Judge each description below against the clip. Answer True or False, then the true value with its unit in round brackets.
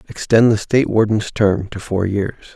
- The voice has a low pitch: True (105 Hz)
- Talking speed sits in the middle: True (190 wpm)